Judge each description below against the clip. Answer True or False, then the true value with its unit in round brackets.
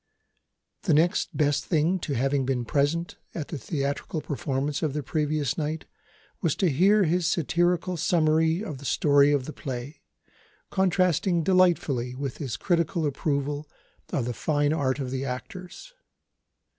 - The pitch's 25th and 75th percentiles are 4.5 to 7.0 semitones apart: False (3.4 semitones)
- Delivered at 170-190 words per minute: False (145 wpm)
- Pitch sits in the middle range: True (150 Hz)